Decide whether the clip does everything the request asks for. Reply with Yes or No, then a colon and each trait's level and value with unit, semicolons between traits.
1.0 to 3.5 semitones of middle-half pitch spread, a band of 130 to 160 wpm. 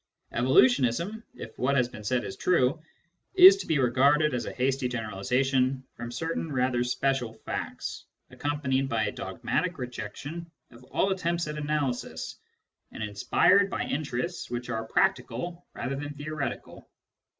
No: average, 4.1 semitones; average, 140 wpm